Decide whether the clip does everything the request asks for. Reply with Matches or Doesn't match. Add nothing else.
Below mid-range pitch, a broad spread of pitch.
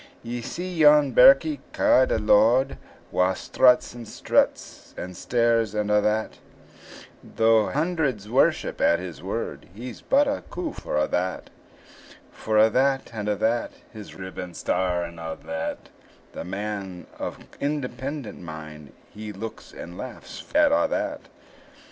Matches